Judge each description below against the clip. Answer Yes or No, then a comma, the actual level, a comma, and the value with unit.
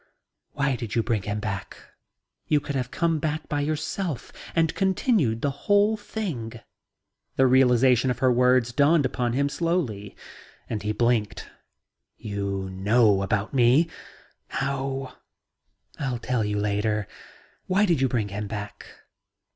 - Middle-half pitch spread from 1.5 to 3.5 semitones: No, wide, 5.4 semitones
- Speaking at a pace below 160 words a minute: Yes, average, 140 wpm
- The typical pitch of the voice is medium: No, low, 125 Hz